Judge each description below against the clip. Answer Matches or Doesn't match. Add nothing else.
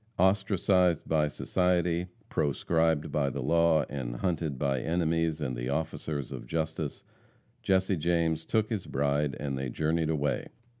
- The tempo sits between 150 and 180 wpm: Doesn't match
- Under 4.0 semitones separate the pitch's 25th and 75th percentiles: Matches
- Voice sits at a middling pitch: Doesn't match